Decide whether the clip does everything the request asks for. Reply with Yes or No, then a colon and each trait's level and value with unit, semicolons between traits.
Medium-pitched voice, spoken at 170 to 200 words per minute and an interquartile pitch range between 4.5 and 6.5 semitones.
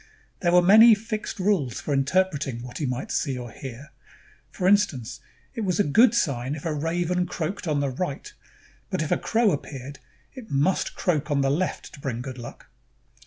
Yes: medium, 150 Hz; average, 190 wpm; wide, 5.5 semitones